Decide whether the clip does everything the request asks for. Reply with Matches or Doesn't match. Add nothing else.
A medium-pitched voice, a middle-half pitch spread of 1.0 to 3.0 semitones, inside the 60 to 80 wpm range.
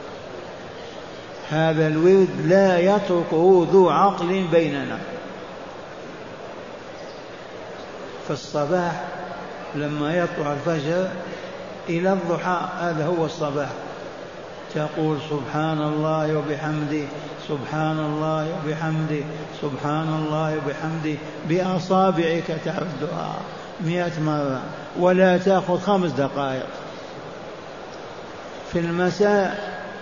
Matches